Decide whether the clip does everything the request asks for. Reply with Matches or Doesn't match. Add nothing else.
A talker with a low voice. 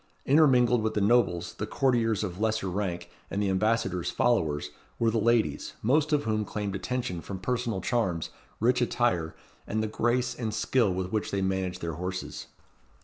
Matches